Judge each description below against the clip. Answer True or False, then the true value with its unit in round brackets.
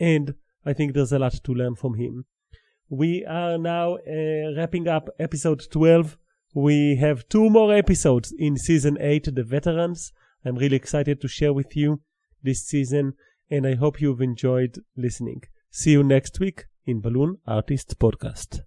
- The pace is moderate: True (165 wpm)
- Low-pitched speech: False (145 Hz)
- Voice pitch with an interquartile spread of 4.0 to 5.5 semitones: False (3.6 semitones)